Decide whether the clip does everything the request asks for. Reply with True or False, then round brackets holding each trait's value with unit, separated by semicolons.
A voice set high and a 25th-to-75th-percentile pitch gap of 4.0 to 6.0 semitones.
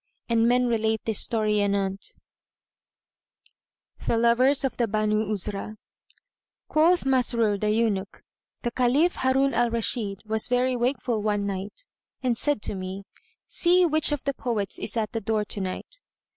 False (225 Hz; 3.4 semitones)